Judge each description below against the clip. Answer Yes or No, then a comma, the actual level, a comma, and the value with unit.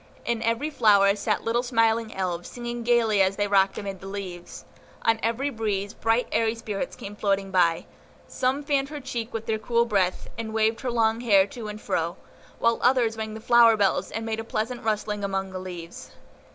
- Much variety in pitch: No, average, 2.8 semitones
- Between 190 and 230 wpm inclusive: Yes, average, 195 wpm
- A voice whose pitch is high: Yes, high, 220 Hz